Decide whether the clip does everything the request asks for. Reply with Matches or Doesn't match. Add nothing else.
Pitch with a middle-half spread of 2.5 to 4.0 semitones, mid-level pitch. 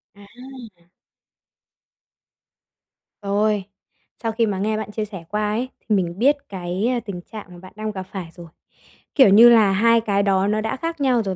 Doesn't match